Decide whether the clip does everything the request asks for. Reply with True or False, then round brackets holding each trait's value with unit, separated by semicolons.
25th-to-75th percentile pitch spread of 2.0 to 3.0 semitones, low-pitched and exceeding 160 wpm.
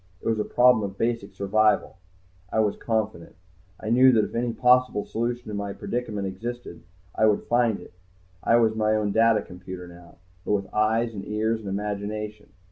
True (2.4 semitones; 110 Hz; 185 wpm)